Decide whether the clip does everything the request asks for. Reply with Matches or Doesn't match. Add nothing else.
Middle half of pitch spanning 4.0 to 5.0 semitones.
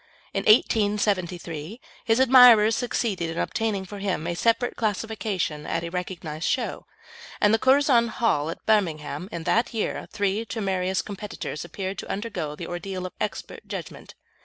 Matches